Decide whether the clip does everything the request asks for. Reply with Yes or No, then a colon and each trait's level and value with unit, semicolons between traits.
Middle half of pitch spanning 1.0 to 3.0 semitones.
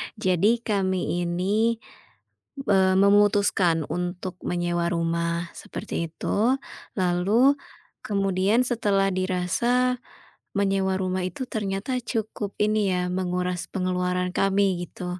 Yes: narrow, 2.5 semitones